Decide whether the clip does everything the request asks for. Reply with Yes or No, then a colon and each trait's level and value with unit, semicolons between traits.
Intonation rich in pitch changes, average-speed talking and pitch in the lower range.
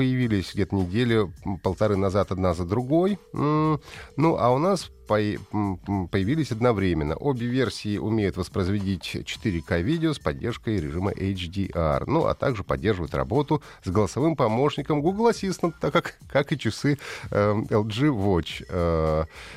Yes: wide, 6.9 semitones; average, 130 wpm; low, 105 Hz